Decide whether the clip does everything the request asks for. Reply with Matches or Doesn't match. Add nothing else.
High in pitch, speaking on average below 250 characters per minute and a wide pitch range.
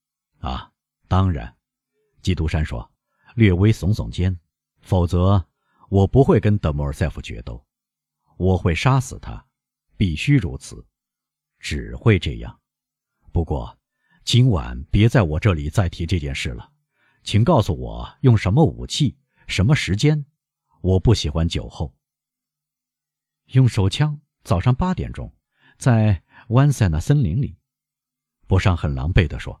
Doesn't match